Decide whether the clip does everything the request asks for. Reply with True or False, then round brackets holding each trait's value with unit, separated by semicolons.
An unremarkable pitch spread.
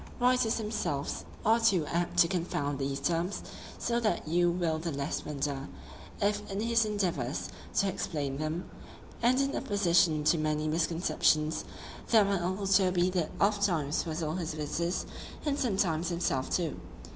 True (4.6 semitones)